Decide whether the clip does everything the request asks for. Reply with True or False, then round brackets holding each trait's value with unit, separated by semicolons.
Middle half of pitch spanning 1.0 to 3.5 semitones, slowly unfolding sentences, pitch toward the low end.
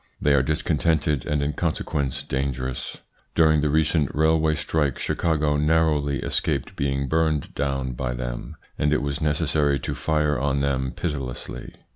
False (2.4 semitones; 145 wpm; 75 Hz)